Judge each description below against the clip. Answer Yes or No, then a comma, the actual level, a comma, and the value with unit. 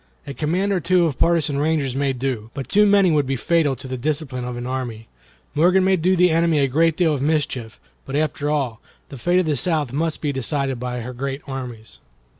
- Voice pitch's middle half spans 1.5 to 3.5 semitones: No, average, 4.1 semitones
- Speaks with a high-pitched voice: No, medium, 145 Hz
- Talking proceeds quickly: Yes, fast, 225 wpm